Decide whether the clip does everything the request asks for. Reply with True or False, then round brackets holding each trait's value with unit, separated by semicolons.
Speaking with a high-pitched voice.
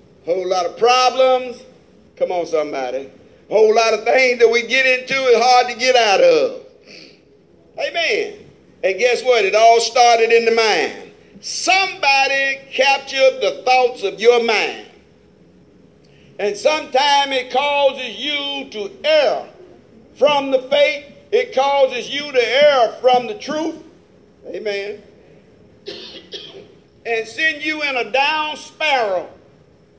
True (265 Hz)